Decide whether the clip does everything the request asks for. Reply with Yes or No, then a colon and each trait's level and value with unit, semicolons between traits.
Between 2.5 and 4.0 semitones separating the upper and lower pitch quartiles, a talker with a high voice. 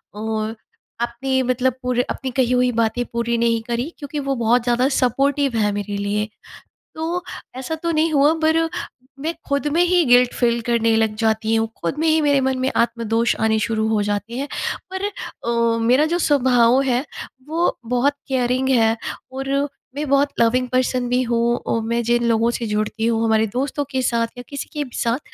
Yes: average, 3.1 semitones; high, 245 Hz